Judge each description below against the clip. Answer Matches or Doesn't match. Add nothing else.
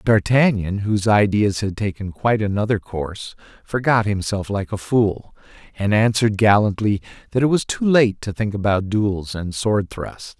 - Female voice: Doesn't match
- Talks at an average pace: Matches